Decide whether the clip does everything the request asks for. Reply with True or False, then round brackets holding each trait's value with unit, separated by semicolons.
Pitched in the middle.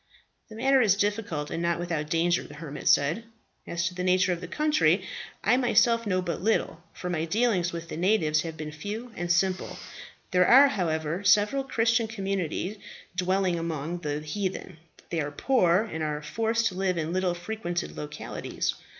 True (180 Hz)